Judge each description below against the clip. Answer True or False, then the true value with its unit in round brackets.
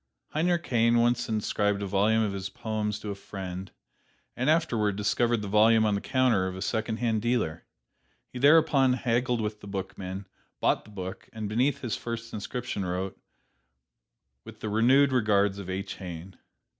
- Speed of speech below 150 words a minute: False (165 wpm)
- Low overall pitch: True (110 Hz)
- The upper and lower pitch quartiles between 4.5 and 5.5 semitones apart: False (3.4 semitones)